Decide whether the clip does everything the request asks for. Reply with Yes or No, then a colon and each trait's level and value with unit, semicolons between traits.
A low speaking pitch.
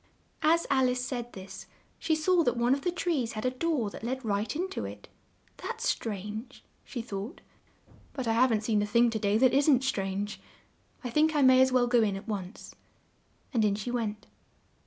No: high, 240 Hz